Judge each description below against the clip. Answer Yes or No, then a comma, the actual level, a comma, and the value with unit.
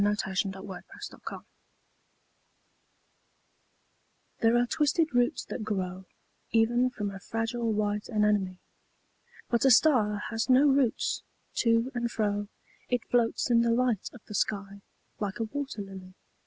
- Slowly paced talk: Yes, slow, 130 wpm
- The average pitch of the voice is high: Yes, high, 225 Hz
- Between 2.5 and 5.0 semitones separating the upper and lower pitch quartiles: Yes, average, 3.0 semitones